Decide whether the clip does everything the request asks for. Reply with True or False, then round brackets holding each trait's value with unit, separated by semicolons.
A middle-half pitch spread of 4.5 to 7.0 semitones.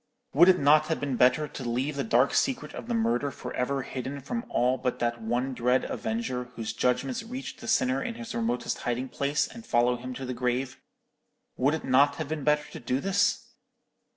False (4.1 semitones)